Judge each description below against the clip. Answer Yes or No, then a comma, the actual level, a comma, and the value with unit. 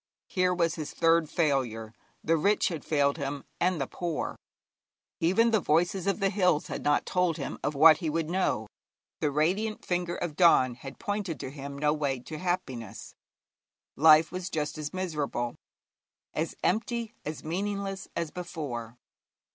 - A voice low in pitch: No, medium, 160 Hz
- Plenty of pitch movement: No, average, 4.1 semitones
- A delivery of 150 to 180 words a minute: Yes, average, 160 wpm